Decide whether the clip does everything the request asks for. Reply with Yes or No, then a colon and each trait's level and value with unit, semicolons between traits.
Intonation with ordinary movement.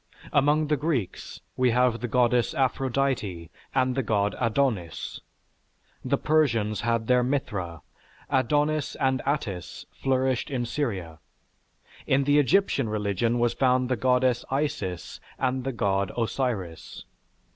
Yes: average, 4.1 semitones